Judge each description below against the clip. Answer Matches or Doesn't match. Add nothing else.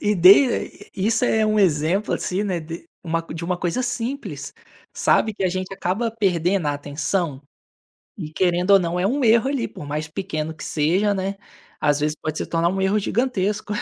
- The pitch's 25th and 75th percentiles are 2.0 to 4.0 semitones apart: Doesn't match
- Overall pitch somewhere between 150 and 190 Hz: Matches